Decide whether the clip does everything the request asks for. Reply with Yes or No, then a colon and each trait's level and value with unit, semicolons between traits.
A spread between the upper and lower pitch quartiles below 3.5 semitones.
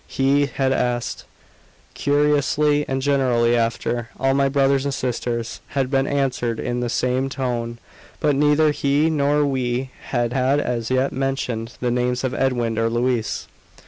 Yes: narrow, 2.4 semitones